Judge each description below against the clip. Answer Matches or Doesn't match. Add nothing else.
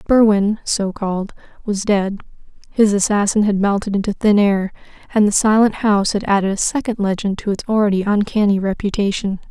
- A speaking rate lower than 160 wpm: Matches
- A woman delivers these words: Matches